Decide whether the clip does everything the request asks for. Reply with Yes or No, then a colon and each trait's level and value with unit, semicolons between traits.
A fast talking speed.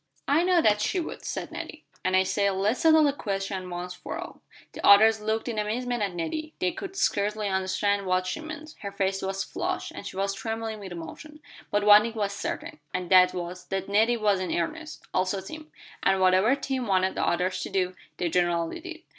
Yes: fast, 210 wpm